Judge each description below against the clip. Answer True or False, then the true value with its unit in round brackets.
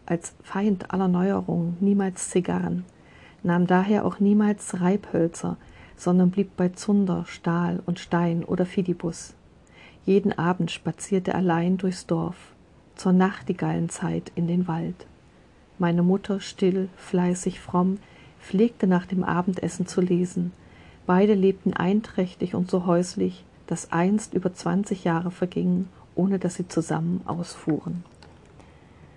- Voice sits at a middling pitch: True (180 Hz)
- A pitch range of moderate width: False (2.0 semitones)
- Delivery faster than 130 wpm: False (120 wpm)